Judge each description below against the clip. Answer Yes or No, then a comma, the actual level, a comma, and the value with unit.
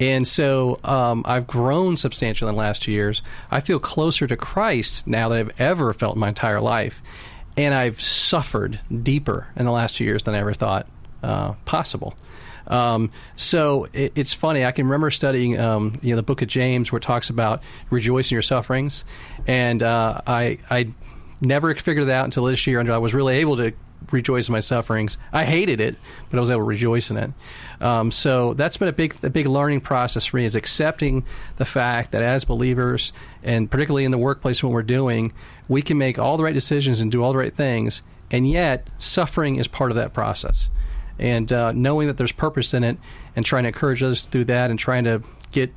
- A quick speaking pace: Yes, fast, 215 wpm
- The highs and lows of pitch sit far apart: No, average, 3.0 semitones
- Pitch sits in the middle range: No, low, 125 Hz